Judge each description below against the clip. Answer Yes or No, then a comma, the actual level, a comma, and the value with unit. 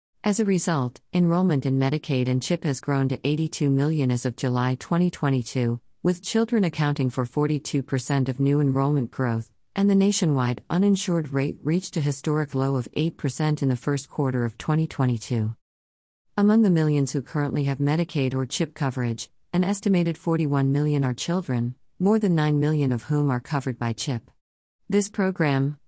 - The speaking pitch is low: No, medium, 145 Hz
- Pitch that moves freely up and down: No, average, 4.4 semitones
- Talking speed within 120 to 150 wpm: No, average, 165 wpm